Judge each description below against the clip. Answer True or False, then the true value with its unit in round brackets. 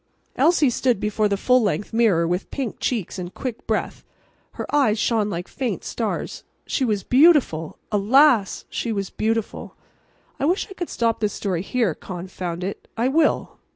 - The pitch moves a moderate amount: True (4.6 semitones)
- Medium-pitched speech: False (220 Hz)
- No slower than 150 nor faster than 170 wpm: True (165 wpm)